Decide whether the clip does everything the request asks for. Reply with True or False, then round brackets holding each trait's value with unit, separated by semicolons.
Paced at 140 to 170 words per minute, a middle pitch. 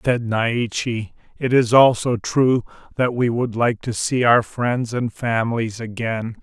False (160 wpm; 120 Hz)